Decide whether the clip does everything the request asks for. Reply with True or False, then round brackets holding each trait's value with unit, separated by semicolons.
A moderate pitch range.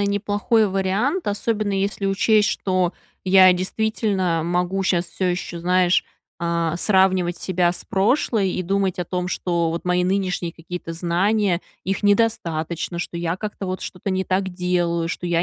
False (2.2 semitones)